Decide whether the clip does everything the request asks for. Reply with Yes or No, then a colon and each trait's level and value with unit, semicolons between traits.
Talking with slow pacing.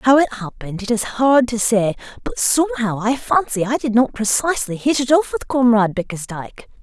No: average, 195 wpm